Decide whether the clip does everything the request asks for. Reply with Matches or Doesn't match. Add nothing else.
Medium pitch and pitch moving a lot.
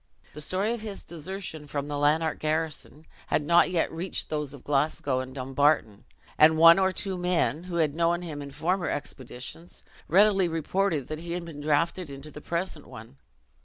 Doesn't match